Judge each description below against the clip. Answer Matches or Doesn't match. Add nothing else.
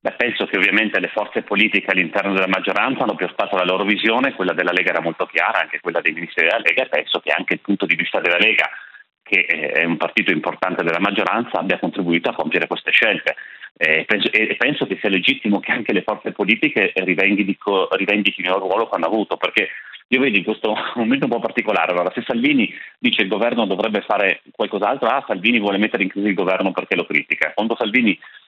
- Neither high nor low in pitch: Doesn't match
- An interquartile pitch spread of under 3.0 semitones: Matches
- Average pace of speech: Doesn't match